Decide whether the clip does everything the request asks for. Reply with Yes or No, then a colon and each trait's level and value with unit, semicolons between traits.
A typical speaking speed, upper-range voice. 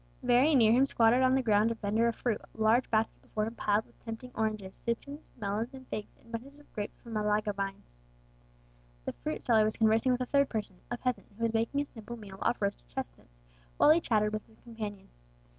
No: fast, 220 wpm; high, 225 Hz